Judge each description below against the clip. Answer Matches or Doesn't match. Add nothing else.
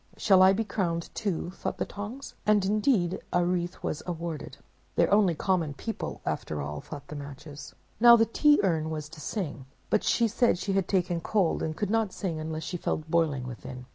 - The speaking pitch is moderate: Matches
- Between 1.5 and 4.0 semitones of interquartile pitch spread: Doesn't match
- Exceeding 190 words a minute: Matches